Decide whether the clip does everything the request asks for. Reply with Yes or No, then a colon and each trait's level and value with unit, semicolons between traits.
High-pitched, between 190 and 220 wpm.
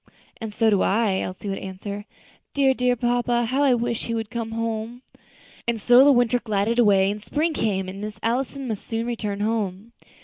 Yes: high, 225 Hz; average, 195 wpm